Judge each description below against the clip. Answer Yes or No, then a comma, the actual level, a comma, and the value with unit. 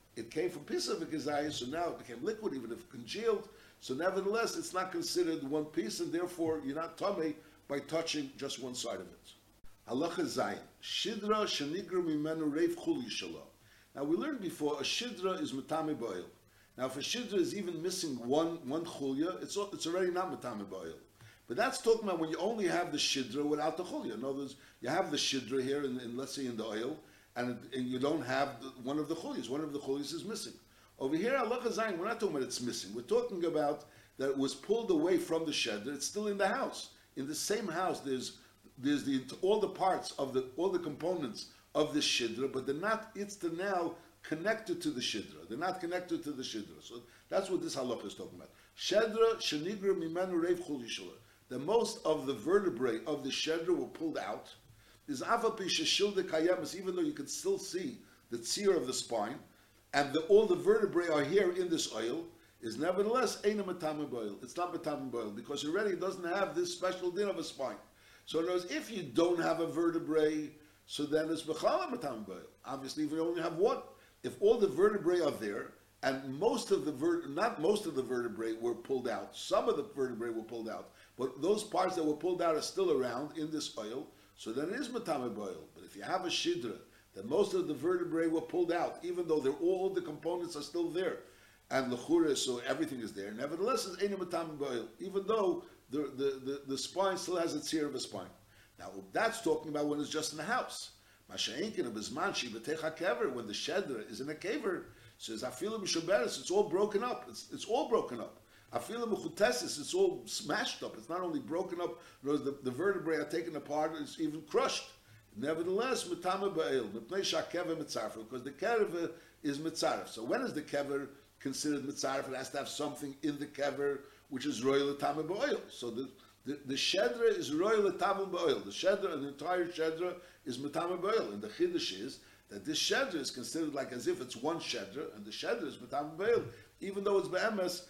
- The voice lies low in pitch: No, medium, 170 Hz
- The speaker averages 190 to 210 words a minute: Yes, average, 195 wpm